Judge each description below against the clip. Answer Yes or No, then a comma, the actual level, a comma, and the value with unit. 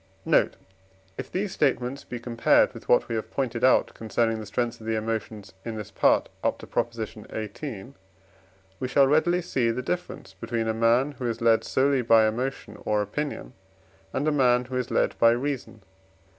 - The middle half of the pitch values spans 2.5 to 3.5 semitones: Yes, average, 3.1 semitones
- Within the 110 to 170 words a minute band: No, average, 185 wpm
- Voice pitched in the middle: No, low, 120 Hz